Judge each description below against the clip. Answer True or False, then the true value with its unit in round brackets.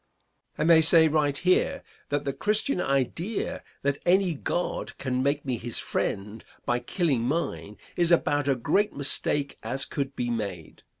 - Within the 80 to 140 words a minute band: False (160 wpm)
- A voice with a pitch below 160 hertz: True (140 Hz)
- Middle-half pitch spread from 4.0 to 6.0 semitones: True (5.2 semitones)